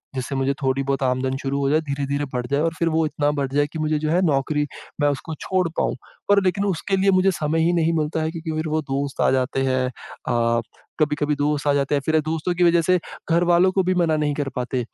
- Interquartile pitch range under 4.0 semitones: Yes, average, 3.2 semitones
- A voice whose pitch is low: No, medium, 150 Hz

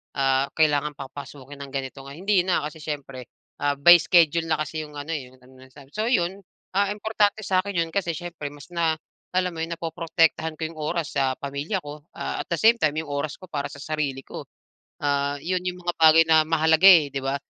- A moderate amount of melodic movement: Yes, average, 3.4 semitones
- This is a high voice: No, medium, 155 Hz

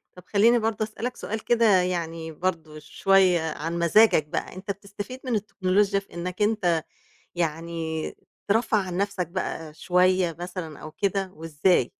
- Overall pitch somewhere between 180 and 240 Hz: Yes, medium, 185 Hz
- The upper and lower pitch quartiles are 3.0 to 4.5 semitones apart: Yes, average, 3.7 semitones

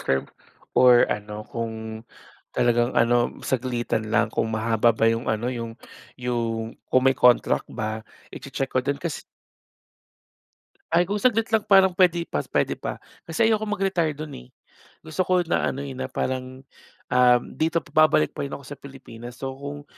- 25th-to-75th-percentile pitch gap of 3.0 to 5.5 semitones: Yes, average, 5.2 semitones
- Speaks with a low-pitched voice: Yes, low, 130 Hz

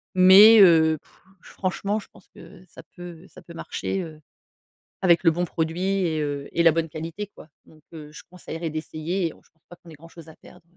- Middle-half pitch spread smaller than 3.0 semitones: Yes, narrow, 2.5 semitones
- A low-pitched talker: No, medium, 170 Hz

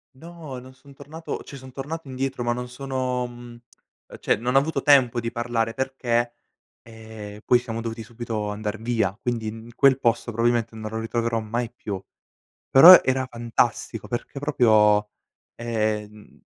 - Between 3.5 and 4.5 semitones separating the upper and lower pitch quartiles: No, average, 2.7 semitones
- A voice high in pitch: No, low, 120 Hz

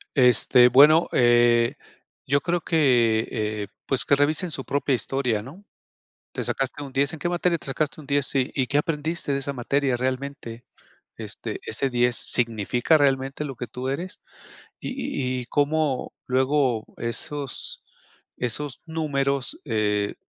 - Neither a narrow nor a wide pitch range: Yes, average, 3.1 semitones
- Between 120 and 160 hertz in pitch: Yes, low, 135 Hz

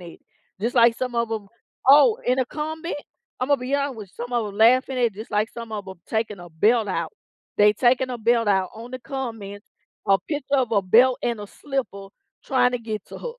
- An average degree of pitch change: Yes, average, 3.6 semitones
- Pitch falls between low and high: No, high, 235 Hz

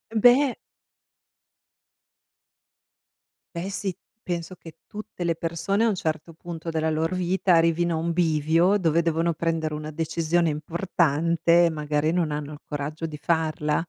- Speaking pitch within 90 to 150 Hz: No, medium, 165 Hz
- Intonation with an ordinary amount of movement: No, narrow, 1.8 semitones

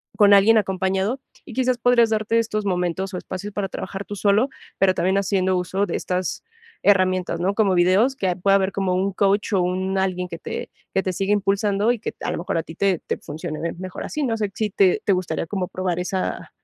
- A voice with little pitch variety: Yes, narrow, 2.1 semitones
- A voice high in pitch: Yes, high, 195 Hz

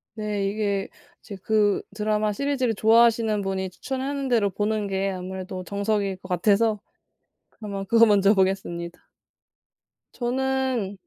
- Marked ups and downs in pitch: No, average, 2.7 semitones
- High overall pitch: Yes, high, 210 Hz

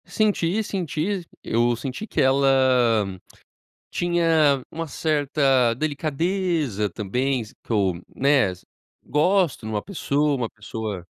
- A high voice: No, medium, 140 Hz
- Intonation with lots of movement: Yes, wide, 5.8 semitones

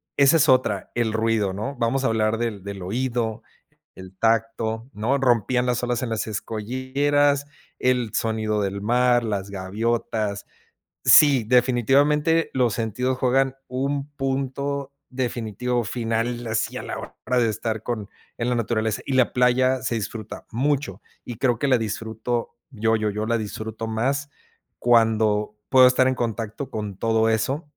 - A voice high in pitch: No, low, 120 Hz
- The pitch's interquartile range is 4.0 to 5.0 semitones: No, average, 2.8 semitones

